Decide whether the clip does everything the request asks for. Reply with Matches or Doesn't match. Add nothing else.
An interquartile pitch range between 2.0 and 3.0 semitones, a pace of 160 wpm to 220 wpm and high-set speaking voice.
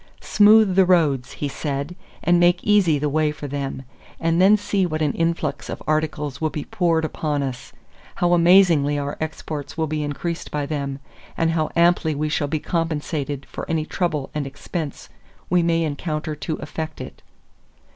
Doesn't match